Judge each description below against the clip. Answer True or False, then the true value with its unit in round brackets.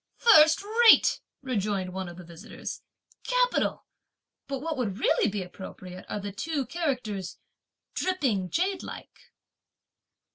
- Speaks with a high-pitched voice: True (240 Hz)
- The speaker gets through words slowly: True (120 wpm)